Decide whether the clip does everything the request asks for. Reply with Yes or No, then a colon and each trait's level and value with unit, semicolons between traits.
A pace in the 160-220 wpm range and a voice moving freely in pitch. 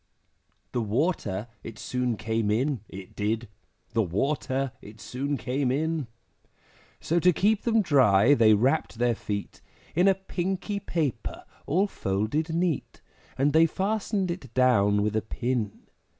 No: average, 140 wpm; wide, 7.1 semitones